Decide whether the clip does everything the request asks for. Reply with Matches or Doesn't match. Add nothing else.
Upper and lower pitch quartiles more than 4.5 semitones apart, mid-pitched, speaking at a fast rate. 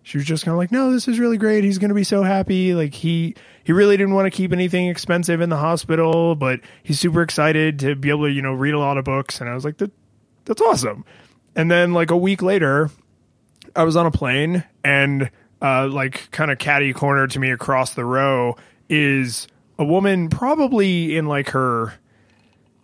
Matches